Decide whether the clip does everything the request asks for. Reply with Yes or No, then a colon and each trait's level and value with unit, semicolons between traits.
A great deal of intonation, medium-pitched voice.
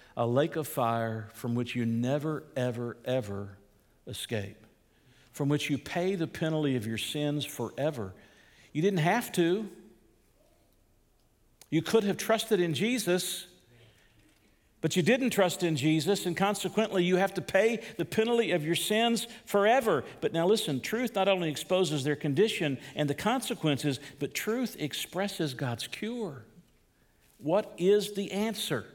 Yes: wide, 7.8 semitones; medium, 160 Hz